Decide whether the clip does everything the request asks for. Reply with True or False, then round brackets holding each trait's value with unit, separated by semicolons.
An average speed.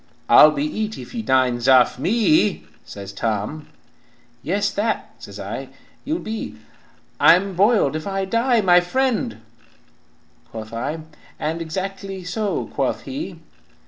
False (130 wpm)